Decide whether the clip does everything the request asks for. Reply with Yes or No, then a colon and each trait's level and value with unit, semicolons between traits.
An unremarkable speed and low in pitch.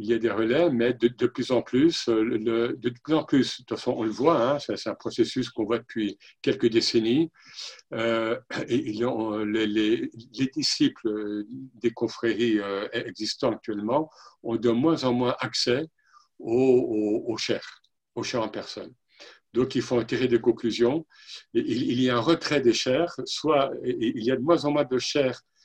Yes: average, 190 wpm; low, 125 Hz